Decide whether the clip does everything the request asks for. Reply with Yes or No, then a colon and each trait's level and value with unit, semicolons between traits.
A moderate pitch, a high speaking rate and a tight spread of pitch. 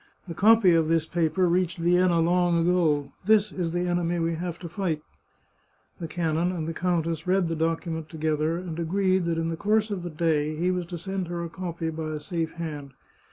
Yes: medium, 170 Hz; fast, 215 wpm; narrow, 1.8 semitones